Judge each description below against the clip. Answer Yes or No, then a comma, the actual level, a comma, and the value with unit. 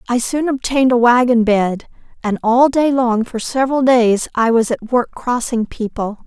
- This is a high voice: Yes, high, 240 Hz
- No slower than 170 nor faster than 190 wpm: Yes, average, 180 wpm